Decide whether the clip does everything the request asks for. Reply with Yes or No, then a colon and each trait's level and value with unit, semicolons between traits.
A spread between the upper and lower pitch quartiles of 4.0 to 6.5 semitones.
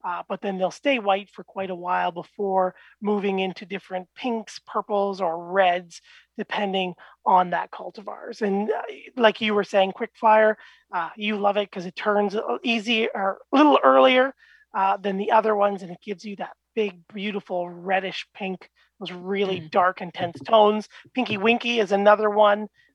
No: narrow, 2.5 semitones